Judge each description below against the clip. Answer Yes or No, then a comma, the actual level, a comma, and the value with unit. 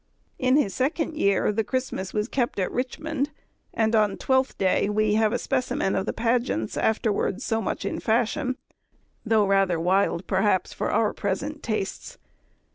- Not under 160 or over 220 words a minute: Yes, average, 165 wpm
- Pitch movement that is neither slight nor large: Yes, average, 4.5 semitones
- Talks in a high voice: Yes, high, 220 Hz